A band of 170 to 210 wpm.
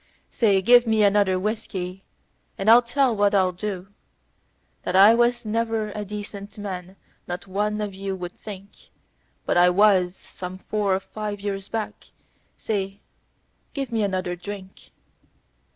No: average, 145 wpm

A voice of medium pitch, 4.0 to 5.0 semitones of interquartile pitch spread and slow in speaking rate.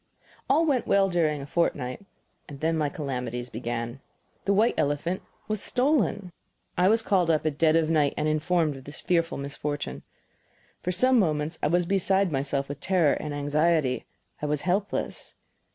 No: medium, 155 Hz; average, 4.4 semitones; average, 165 wpm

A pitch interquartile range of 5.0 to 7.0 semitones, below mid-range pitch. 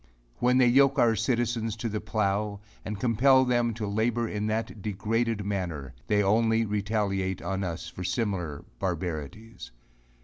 No: average, 2.9 semitones; low, 105 Hz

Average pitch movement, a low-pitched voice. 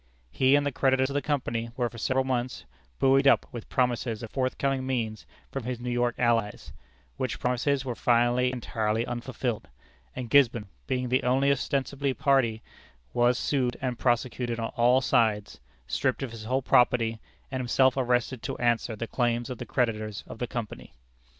No: narrow, 2.1 semitones; low, 125 Hz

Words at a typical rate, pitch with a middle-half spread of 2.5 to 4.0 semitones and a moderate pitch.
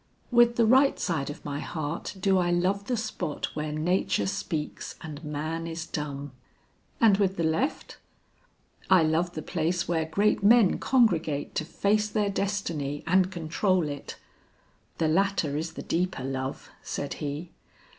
No: average, 155 wpm; average, 4.6 semitones; medium, 170 Hz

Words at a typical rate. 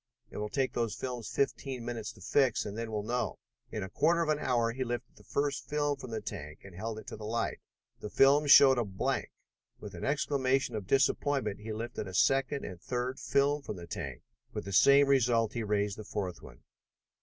No: fast, 215 wpm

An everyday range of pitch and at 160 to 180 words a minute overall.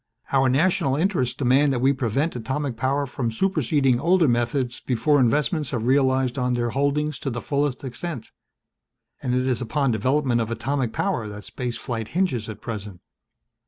Yes: average, 3.2 semitones; average, 165 wpm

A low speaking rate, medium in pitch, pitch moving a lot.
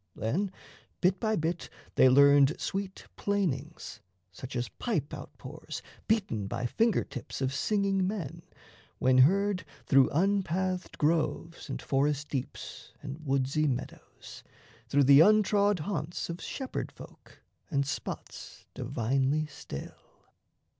Yes: slow, 120 wpm; medium, 155 Hz; wide, 6.0 semitones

